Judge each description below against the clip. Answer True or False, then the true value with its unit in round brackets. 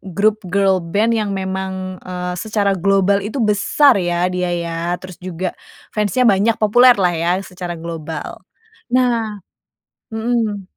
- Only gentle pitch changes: False (3.1 semitones)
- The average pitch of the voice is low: False (200 Hz)